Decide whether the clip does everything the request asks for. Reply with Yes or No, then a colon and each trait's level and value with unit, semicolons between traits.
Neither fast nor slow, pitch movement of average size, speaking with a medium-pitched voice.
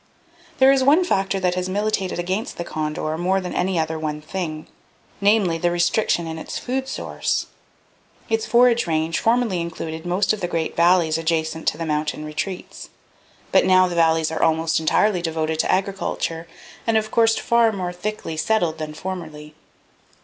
Yes: average, 170 wpm; average, 4.0 semitones; medium, 175 Hz